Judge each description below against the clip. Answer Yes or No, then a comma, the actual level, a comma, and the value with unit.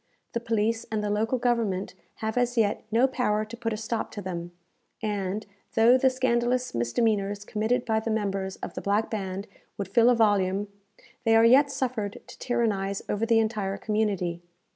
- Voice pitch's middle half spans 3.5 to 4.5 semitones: No, average, 2.8 semitones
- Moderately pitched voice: No, high, 220 Hz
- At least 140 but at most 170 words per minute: No, average, 180 wpm